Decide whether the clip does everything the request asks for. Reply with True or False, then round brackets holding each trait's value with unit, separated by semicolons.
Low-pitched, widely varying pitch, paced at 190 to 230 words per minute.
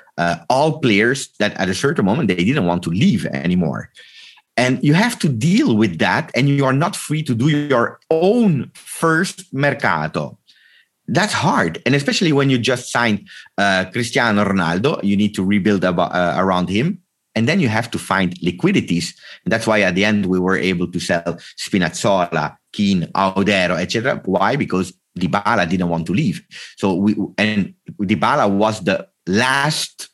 False (110 Hz; 8.1 semitones; 175 wpm)